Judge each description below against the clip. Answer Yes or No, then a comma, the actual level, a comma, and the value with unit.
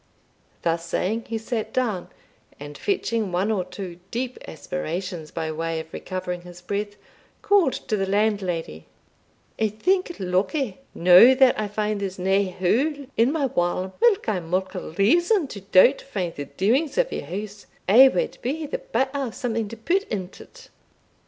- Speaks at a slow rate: No, average, 165 wpm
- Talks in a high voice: Yes, high, 205 Hz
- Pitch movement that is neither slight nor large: No, wide, 6.2 semitones